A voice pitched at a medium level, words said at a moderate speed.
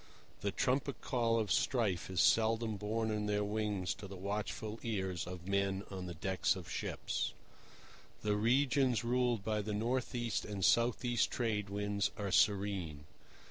No: low, 105 Hz; average, 160 wpm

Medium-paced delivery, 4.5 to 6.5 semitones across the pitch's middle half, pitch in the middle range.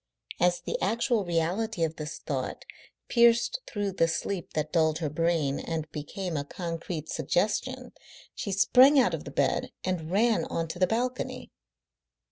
Yes: average, 155 wpm; wide, 5.6 semitones; medium, 175 Hz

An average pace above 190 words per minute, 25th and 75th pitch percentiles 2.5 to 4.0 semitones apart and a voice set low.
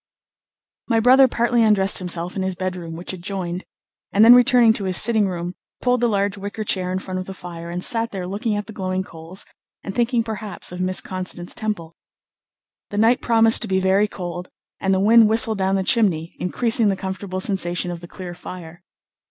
No: average, 200 wpm; average, 3.4 semitones; high, 195 Hz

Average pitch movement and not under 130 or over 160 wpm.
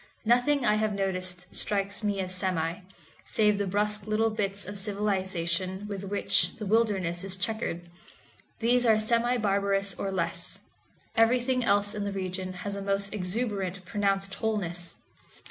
No: narrow, 2.2 semitones; average, 145 wpm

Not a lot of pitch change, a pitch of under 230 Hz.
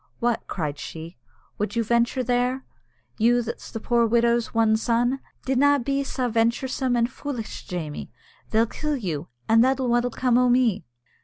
No: narrow, 2.1 semitones; high, 235 Hz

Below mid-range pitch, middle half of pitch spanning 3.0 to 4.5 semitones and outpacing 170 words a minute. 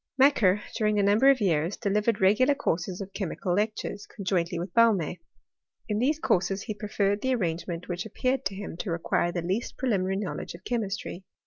No: high, 200 Hz; average, 3.3 semitones; average, 195 wpm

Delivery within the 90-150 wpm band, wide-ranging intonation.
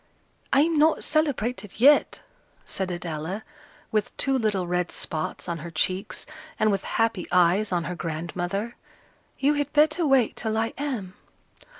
Yes: average, 140 wpm; wide, 7.2 semitones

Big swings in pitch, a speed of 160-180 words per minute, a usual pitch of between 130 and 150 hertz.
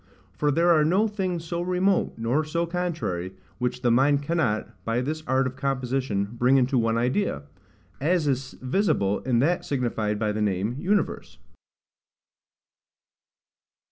No: wide, 6.2 semitones; average, 140 wpm; low, 135 Hz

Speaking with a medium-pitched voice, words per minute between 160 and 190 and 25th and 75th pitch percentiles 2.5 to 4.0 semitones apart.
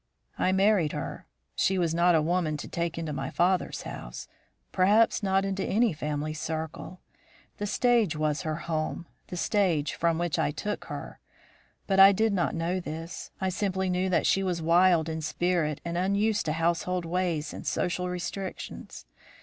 Yes: medium, 175 Hz; average, 170 wpm; average, 2.9 semitones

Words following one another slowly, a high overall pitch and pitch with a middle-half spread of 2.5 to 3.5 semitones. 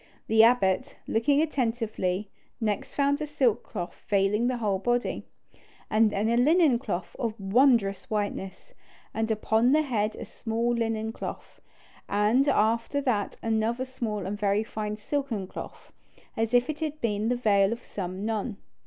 No: average, 155 wpm; high, 225 Hz; average, 3.0 semitones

